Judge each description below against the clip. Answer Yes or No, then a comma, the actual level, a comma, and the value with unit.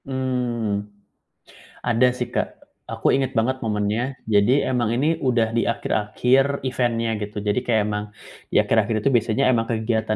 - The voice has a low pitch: Yes, low, 115 Hz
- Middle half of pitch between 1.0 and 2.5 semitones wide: No, average, 2.9 semitones